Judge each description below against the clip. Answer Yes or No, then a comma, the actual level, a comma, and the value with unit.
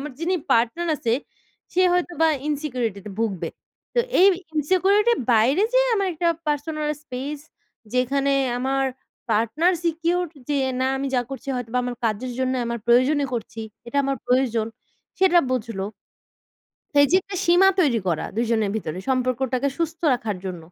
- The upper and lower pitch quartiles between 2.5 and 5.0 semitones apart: No, wide, 5.6 semitones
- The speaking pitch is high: Yes, very high, 270 Hz